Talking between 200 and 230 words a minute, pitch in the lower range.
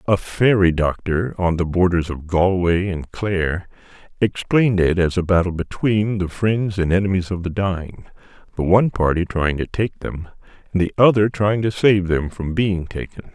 No: average, 175 wpm; very low, 95 Hz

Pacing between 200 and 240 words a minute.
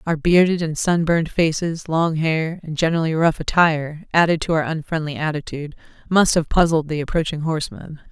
No: average, 170 wpm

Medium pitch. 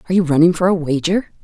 Yes: medium, 170 Hz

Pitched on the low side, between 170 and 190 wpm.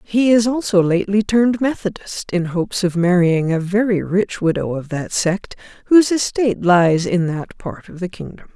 No: high, 195 Hz; average, 180 wpm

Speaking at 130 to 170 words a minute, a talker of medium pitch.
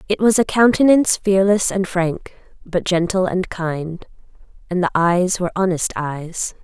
Yes: average, 155 wpm; medium, 180 Hz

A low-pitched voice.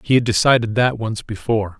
Yes: low, 110 Hz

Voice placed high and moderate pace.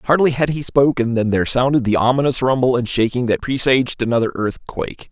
No: low, 125 Hz; average, 190 wpm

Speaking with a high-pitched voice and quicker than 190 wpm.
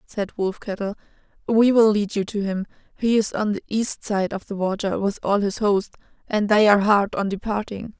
Yes: high, 205 Hz; fast, 205 wpm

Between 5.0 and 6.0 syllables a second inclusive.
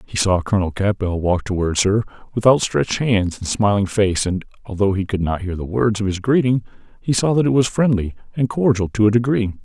Yes: 5.6 syllables/s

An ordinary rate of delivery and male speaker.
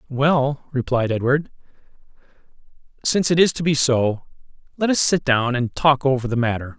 Yes: average, 160 wpm; male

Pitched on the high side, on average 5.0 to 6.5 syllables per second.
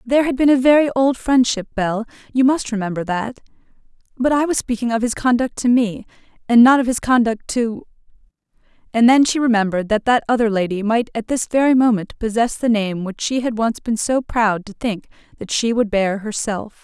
Yes: high, 230 Hz; 5.5 syllables/s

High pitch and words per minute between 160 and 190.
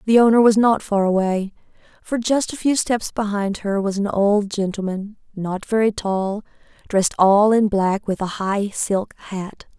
Yes: high, 205 Hz; average, 180 wpm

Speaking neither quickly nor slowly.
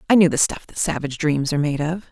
No: fast, 285 wpm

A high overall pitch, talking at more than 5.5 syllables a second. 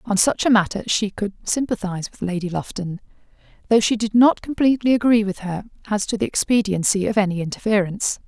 Yes: high, 205 Hz; 6.1 syllables/s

